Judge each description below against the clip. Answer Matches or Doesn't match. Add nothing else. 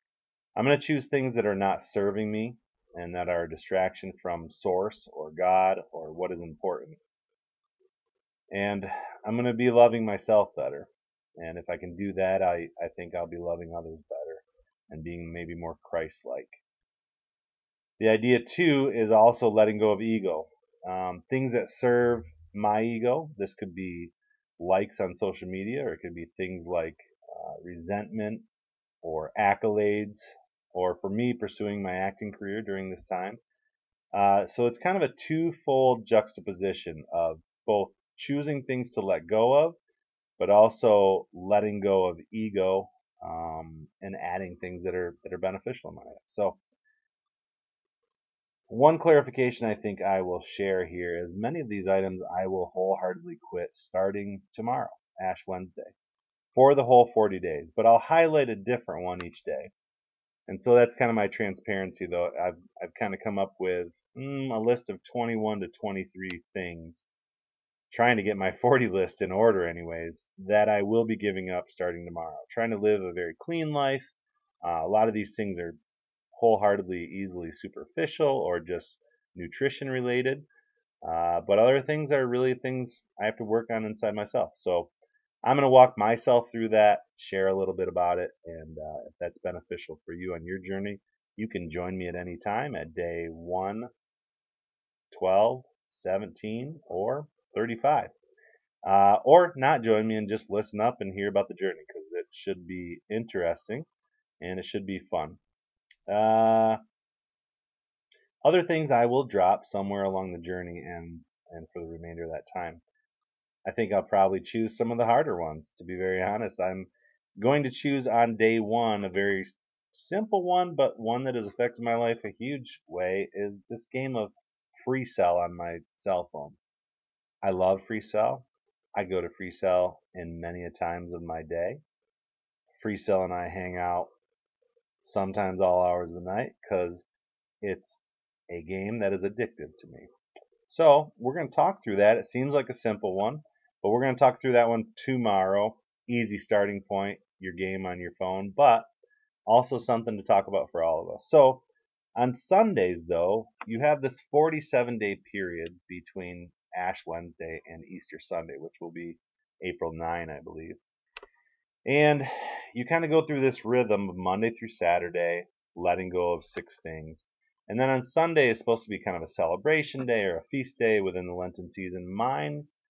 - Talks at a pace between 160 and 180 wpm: Matches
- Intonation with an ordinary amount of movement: Doesn't match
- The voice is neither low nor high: Doesn't match